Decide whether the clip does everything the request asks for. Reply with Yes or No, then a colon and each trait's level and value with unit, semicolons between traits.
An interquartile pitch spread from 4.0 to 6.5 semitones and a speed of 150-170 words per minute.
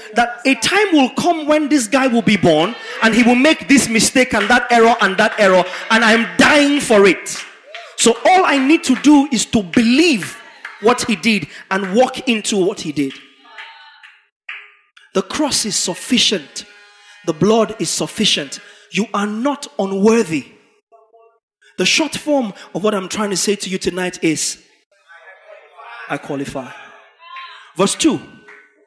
Yes: average, 5.3 semitones; average, 155 wpm